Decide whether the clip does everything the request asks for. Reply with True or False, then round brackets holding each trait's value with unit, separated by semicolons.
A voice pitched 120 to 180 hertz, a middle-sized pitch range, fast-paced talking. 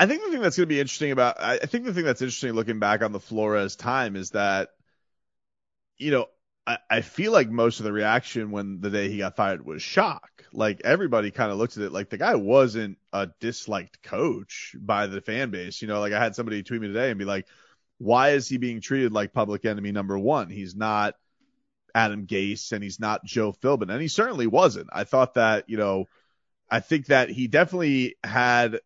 False (110 Hz; 3.7 semitones; 220 wpm)